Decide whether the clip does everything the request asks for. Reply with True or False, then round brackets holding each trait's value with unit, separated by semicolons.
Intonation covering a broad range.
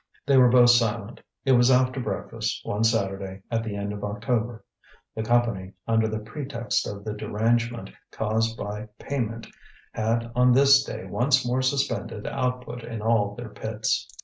False (2.5 semitones)